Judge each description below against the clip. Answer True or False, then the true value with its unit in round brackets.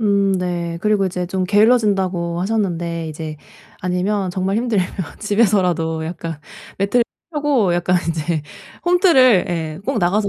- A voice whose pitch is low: False (185 Hz)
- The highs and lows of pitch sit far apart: False (3.5 semitones)